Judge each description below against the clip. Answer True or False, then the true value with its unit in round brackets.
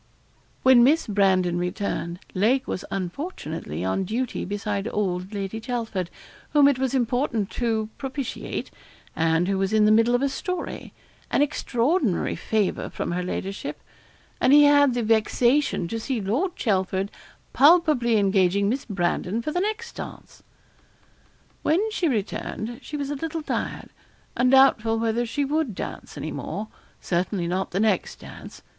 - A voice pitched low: False (225 Hz)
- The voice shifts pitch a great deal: True (5.8 semitones)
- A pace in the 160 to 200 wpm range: False (150 wpm)